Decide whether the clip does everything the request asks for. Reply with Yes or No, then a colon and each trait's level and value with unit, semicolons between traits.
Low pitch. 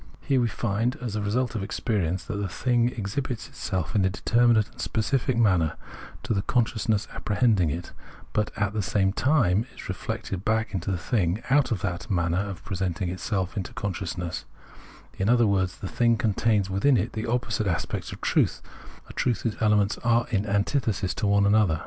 Yes: low, 105 Hz